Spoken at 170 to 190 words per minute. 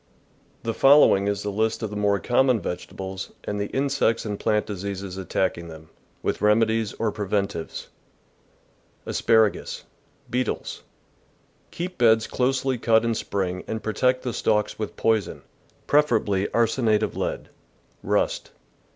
No: average, 150 wpm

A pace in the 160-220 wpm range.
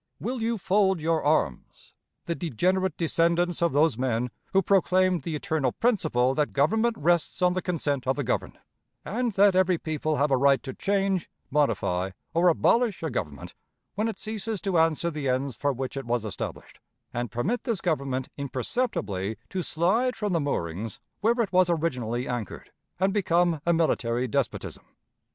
Yes: average, 170 wpm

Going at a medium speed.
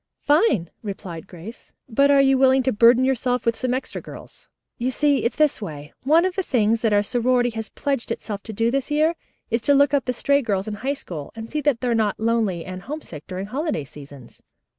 No: fast, 225 wpm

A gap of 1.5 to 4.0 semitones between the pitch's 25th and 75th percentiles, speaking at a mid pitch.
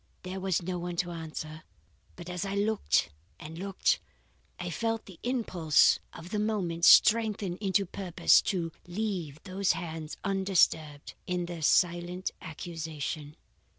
Yes: average, 3.2 semitones; medium, 180 Hz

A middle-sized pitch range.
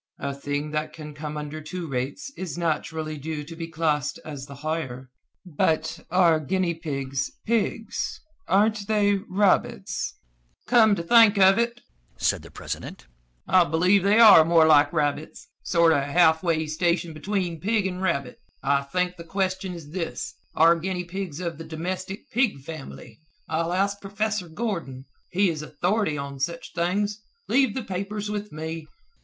Yes: average, 4.3 semitones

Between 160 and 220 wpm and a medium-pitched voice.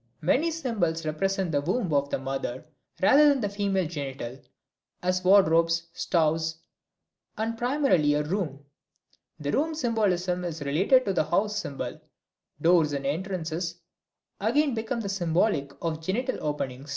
No: average, 140 wpm; medium, 175 Hz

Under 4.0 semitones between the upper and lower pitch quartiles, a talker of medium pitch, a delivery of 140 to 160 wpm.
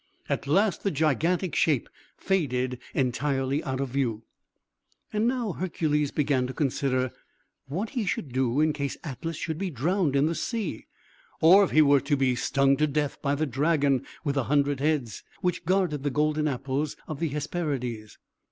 No: average, 3.5 semitones; medium, 145 Hz; average, 170 wpm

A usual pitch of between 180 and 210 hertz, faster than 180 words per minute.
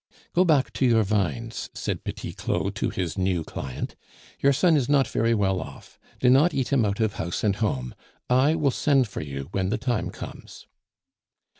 No: low, 115 Hz; average, 190 wpm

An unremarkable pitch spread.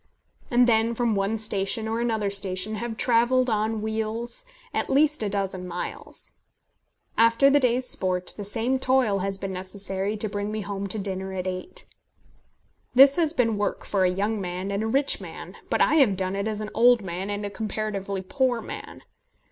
Yes: average, 3.3 semitones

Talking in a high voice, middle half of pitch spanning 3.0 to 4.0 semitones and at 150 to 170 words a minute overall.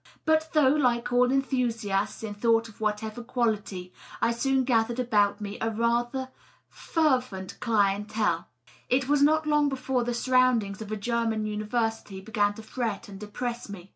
Yes: high, 230 Hz; average, 3.3 semitones; average, 160 wpm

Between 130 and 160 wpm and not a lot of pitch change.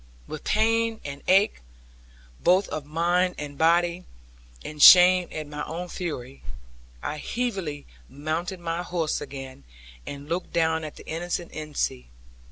No: slow, 135 wpm; average, 3.3 semitones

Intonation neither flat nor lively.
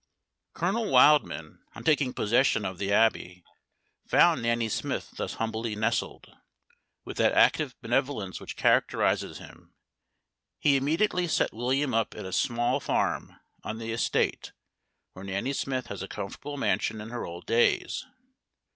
Yes: average, 4.2 semitones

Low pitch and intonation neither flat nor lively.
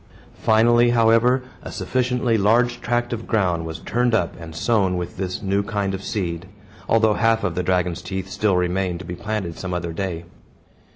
Yes: low, 100 Hz; average, 4.2 semitones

